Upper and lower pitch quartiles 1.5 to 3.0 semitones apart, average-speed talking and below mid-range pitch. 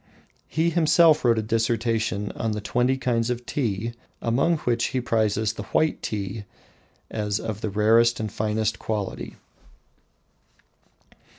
No: narrow, 2.4 semitones; slow, 130 wpm; low, 115 Hz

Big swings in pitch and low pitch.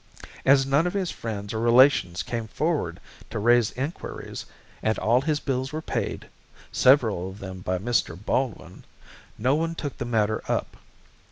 No: average, 5.0 semitones; low, 120 Hz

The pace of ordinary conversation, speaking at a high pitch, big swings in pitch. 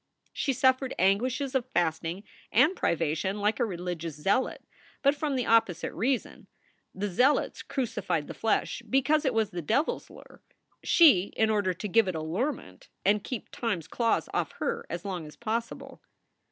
Yes: average, 165 wpm; high, 220 Hz; wide, 6.5 semitones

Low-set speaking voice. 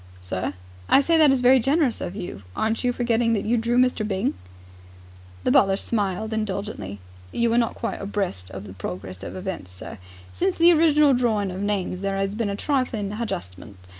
No: high, 210 Hz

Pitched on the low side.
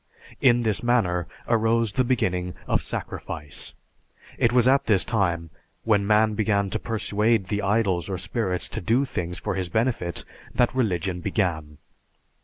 Yes: low, 105 Hz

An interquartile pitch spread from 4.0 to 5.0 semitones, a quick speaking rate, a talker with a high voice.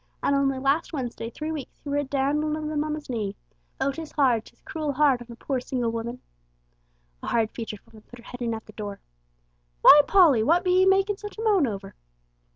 Yes: average, 4.7 semitones; fast, 225 wpm; very high, 275 Hz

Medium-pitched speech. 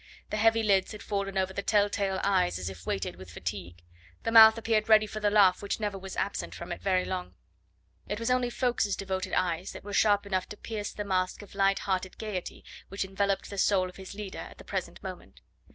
No: high, 200 Hz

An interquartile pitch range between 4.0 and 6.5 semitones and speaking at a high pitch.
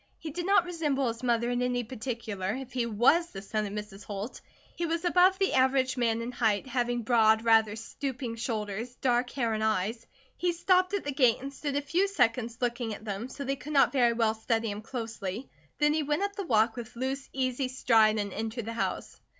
No: average, 3.6 semitones; high, 245 Hz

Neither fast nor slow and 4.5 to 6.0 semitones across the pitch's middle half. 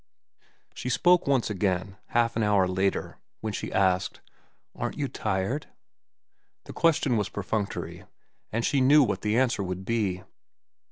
Yes: average, 145 wpm; average, 4.9 semitones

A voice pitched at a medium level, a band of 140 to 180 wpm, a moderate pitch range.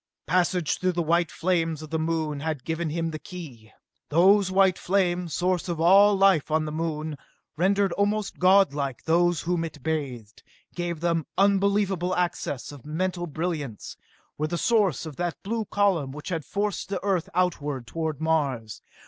Yes: medium, 170 Hz; average, 165 wpm; average, 3.2 semitones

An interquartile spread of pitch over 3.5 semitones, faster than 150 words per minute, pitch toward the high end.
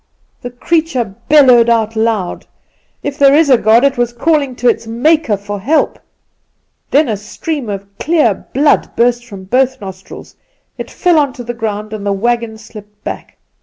Yes: average, 4.7 semitones; average, 165 wpm; high, 240 Hz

